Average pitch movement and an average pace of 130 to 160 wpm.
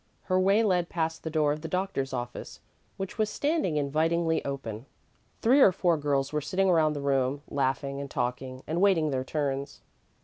No: average, 4.6 semitones; average, 180 wpm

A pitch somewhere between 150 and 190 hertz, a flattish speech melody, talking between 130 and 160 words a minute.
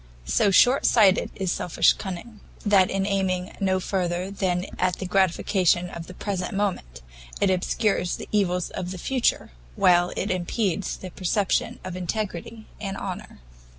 Yes: medium, 185 Hz; narrow, 2.0 semitones; average, 150 wpm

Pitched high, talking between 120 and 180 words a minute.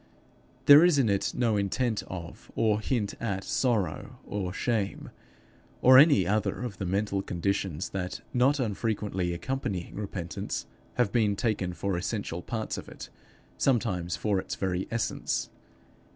No: low, 100 Hz; average, 140 wpm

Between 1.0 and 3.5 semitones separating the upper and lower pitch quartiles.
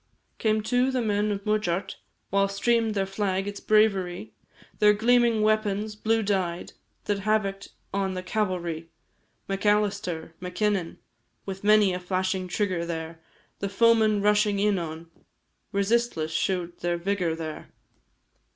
Yes: average, 2.7 semitones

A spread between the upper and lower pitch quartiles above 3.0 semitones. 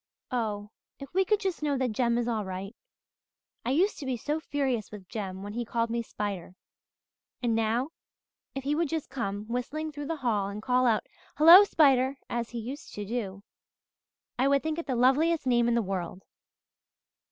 Yes: average, 5.1 semitones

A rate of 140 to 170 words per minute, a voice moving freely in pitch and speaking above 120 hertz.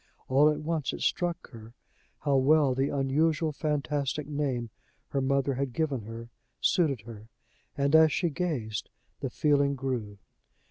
No: average, 145 wpm; average, 3.2 semitones; medium, 140 Hz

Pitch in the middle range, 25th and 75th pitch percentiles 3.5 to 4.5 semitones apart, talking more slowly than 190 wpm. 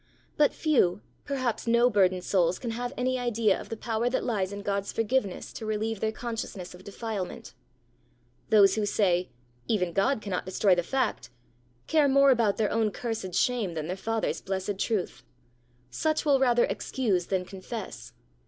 No: high, 215 Hz; average, 4.2 semitones; average, 165 wpm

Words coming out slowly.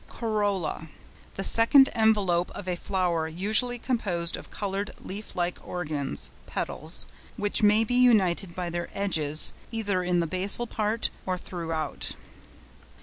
Yes: slow, 130 wpm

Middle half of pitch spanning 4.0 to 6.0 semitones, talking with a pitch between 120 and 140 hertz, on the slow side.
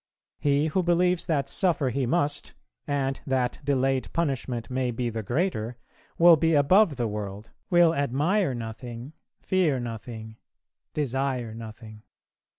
Yes: average, 5.3 semitones; low, 135 Hz; slow, 130 wpm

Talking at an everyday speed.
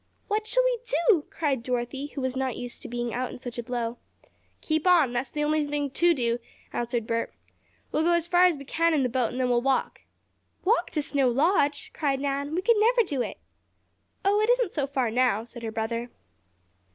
No: fast, 220 wpm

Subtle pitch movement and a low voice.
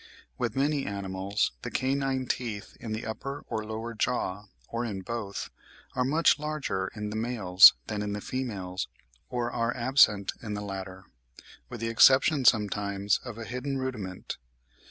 No: average, 4.1 semitones; low, 110 Hz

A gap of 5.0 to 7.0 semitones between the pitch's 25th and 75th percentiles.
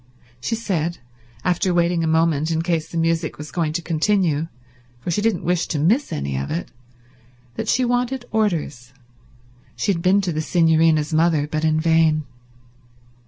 No: narrow, 2.5 semitones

